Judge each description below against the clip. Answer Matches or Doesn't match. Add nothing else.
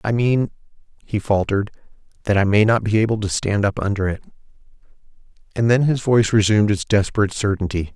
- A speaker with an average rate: Matches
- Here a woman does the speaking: Doesn't match